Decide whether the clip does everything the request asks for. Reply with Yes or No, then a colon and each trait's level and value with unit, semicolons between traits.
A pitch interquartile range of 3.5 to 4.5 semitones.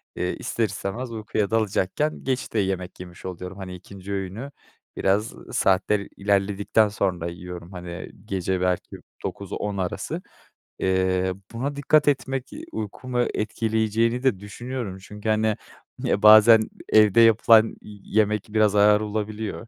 No: average, 2.9 semitones